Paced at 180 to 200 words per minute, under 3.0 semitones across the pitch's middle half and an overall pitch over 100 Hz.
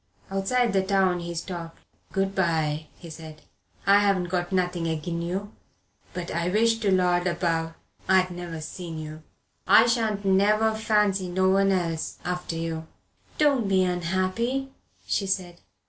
No: average, 145 wpm; narrow, 2.6 semitones; medium, 185 Hz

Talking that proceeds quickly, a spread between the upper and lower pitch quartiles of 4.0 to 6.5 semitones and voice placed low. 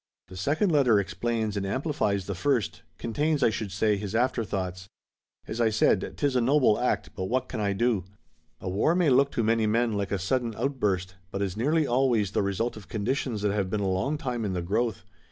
Yes: fast, 215 wpm; average, 4.4 semitones; low, 110 Hz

